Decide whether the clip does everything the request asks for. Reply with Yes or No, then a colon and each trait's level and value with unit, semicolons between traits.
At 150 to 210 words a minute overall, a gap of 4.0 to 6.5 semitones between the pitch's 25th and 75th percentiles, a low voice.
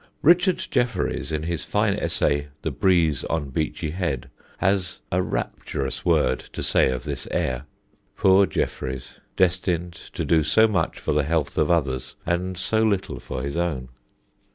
Yes: average, 155 wpm; average, 4.8 semitones; very low, 85 Hz